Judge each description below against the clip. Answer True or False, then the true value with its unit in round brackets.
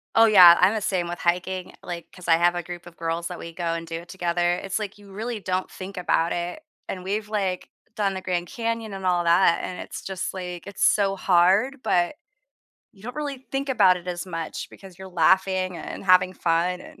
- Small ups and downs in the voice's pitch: True (2.2 semitones)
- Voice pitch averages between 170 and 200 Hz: True (185 Hz)